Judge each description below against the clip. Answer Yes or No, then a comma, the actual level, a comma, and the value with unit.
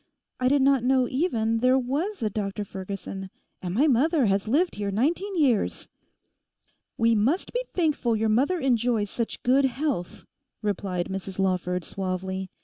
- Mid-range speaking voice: No, high, 230 Hz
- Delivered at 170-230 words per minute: No, average, 150 wpm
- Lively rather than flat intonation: Yes, wide, 5.8 semitones